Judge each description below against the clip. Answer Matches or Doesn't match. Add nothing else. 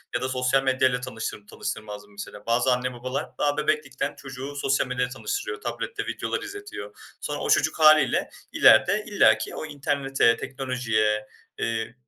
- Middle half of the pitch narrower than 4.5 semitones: Matches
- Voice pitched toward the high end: Doesn't match